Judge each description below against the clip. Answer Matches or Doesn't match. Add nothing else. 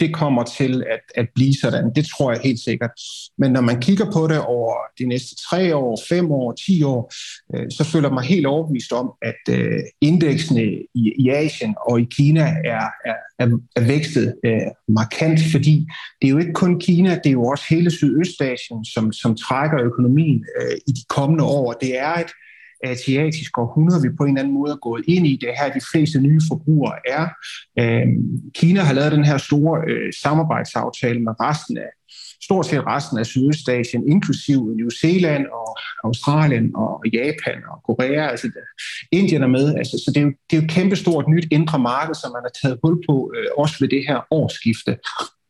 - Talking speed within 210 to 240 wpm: Doesn't match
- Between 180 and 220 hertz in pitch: Doesn't match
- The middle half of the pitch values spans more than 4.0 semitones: Matches